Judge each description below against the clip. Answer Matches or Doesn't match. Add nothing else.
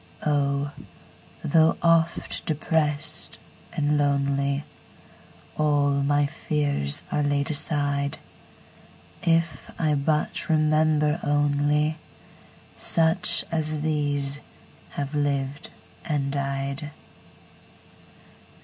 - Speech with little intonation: Matches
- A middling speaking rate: Doesn't match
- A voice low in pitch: Doesn't match